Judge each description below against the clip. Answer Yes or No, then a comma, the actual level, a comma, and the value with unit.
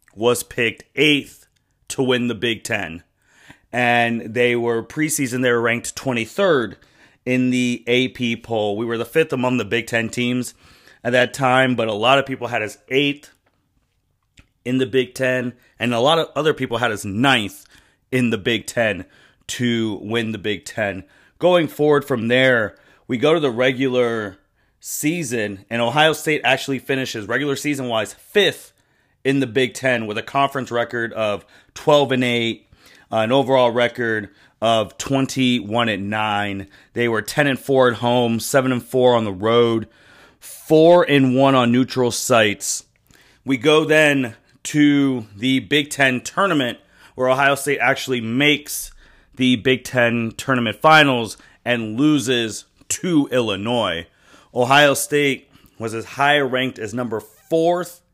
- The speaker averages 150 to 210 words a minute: Yes, average, 155 wpm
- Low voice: Yes, low, 125 Hz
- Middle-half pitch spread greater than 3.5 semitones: No, average, 2.9 semitones